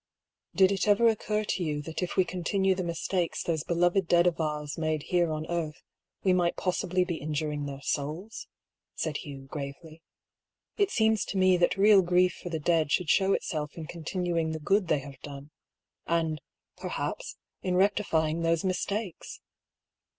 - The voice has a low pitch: No, medium, 170 Hz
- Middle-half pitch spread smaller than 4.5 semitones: Yes, average, 3.3 semitones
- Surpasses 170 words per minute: Yes, average, 180 wpm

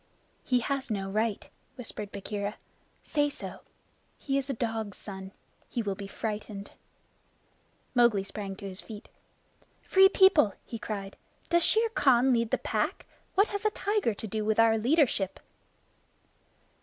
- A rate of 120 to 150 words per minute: Yes, average, 145 wpm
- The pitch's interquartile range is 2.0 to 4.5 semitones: No, average, 5.2 semitones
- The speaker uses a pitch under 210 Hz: No, high, 225 Hz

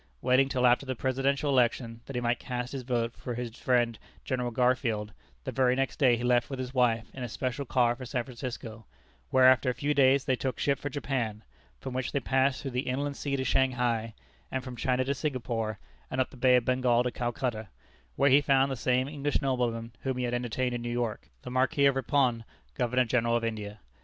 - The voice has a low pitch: Yes, low, 125 Hz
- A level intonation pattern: Yes, narrow, 1.8 semitones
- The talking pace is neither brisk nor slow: No, fast, 220 wpm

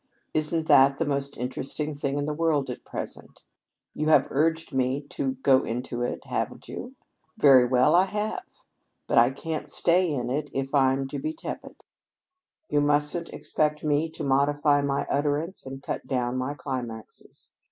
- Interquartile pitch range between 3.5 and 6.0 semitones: No, narrow, 2.6 semitones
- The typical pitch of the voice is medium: Yes, medium, 145 Hz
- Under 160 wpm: No, average, 165 wpm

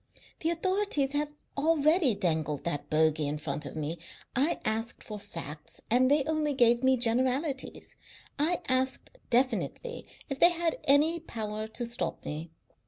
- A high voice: Yes, very high, 255 Hz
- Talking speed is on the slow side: No, average, 150 wpm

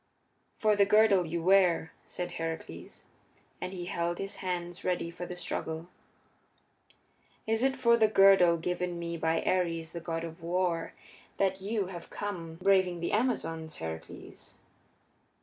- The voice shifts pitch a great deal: No, average, 2.8 semitones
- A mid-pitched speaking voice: Yes, medium, 175 Hz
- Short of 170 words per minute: Yes, average, 145 wpm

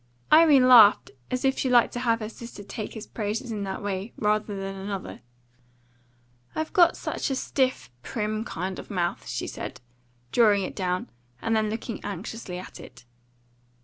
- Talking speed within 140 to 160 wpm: No, average, 170 wpm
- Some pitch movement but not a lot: Yes, average, 3.7 semitones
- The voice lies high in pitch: Yes, high, 215 Hz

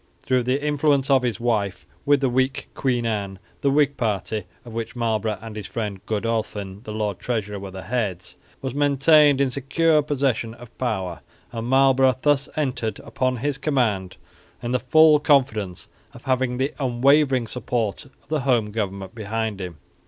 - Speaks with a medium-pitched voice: No, low, 120 Hz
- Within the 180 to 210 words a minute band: No, average, 165 wpm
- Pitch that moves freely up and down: No, average, 4.2 semitones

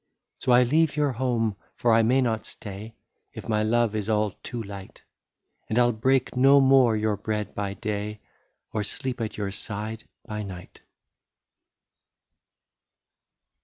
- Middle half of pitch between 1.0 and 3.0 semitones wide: Yes, narrow, 2.6 semitones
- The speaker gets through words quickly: No, average, 165 wpm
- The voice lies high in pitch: No, low, 110 Hz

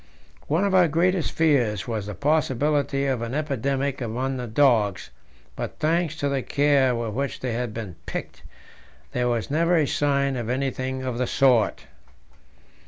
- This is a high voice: No, low, 135 Hz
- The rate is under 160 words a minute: No, average, 165 wpm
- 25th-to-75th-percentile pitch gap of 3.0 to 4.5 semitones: Yes, average, 3.5 semitones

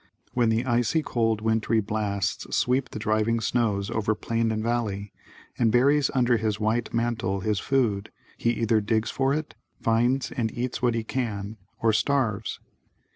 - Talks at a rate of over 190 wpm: No, average, 160 wpm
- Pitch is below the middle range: Yes, low, 115 Hz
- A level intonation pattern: Yes, narrow, 2.0 semitones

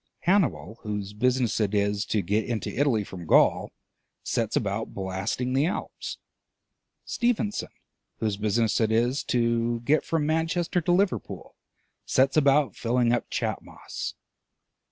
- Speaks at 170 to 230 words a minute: No, slow, 135 wpm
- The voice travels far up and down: Yes, wide, 5.8 semitones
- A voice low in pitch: Yes, low, 120 Hz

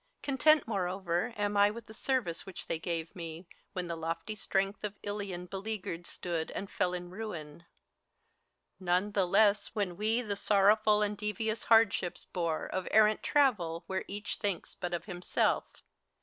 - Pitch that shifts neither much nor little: Yes, average, 3.3 semitones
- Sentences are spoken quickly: No, average, 175 wpm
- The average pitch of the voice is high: Yes, high, 195 Hz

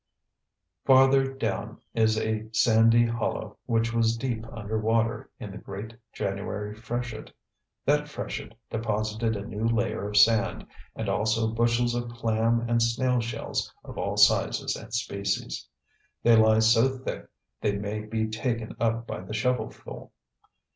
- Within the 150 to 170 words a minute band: No, average, 140 wpm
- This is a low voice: Yes, low, 115 Hz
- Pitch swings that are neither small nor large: No, narrow, 1.4 semitones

